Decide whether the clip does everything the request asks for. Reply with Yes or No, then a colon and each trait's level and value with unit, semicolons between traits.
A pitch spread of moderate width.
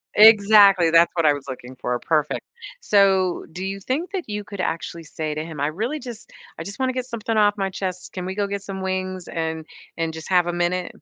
Yes: average, 4.0 semitones